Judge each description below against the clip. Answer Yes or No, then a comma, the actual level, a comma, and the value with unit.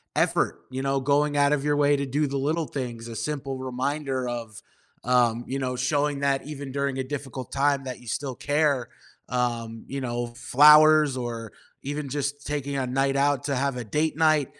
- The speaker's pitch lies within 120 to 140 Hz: Yes, low, 135 Hz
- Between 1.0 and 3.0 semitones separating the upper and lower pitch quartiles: Yes, narrow, 2.4 semitones